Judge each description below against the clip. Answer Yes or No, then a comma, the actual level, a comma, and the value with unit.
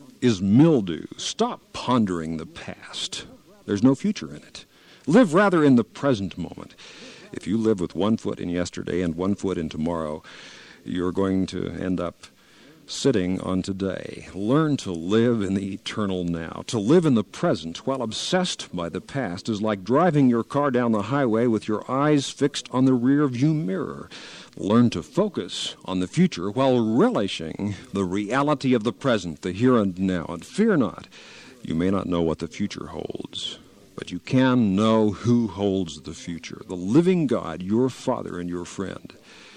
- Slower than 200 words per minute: Yes, average, 175 wpm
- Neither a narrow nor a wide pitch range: No, wide, 6.1 semitones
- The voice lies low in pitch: Yes, low, 105 Hz